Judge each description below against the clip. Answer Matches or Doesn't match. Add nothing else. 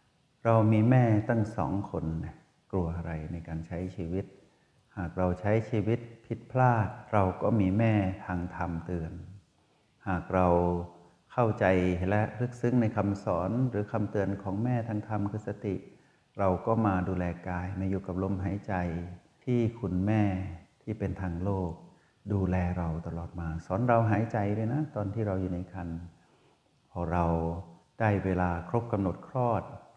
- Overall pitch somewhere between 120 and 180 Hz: Doesn't match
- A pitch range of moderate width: Matches